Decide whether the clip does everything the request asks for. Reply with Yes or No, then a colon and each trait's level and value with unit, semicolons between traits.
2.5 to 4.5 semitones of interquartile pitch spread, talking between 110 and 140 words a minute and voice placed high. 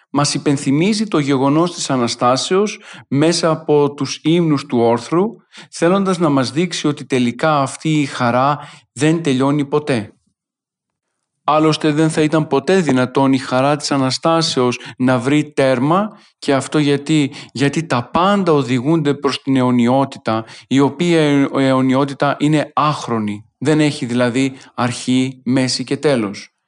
No: average, 3.1 semitones; average, 135 wpm; medium, 140 Hz